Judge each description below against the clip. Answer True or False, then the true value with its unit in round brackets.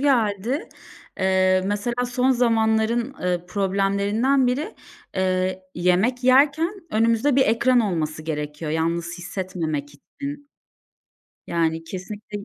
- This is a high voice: True (200 Hz)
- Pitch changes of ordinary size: False (5.7 semitones)